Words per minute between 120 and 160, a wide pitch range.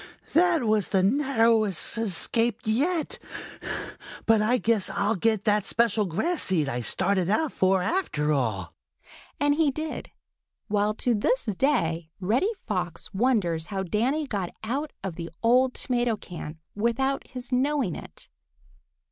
Yes: average, 140 wpm; wide, 5.7 semitones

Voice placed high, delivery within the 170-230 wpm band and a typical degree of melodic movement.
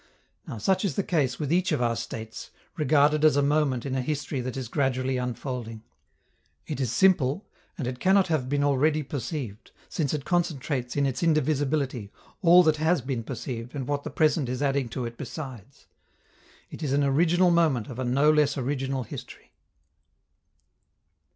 No: medium, 140 Hz; average, 175 wpm; average, 3.4 semitones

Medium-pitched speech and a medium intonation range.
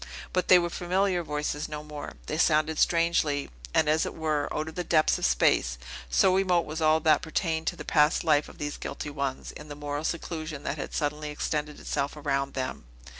No: medium, 155 Hz; narrow, 1.8 semitones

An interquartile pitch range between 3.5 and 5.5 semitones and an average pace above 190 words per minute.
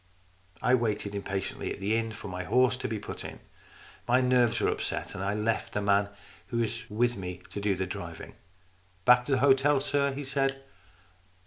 Yes: average, 4.2 semitones; fast, 205 wpm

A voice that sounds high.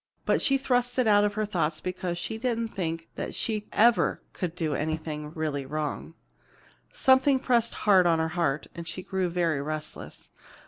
No: medium, 180 Hz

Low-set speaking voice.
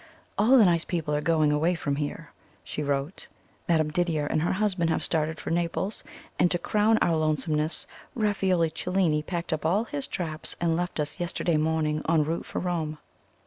No: medium, 165 Hz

